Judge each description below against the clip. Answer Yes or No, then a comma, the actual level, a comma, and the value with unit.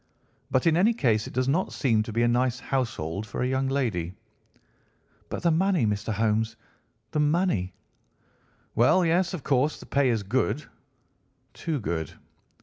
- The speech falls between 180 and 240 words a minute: No, average, 155 wpm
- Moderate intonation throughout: No, wide, 5.9 semitones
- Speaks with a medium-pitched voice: No, low, 125 Hz